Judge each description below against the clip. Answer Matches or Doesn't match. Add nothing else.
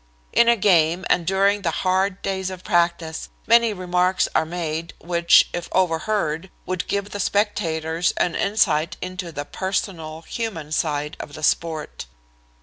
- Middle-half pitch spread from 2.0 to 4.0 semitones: Matches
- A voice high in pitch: Doesn't match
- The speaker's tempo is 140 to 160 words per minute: Matches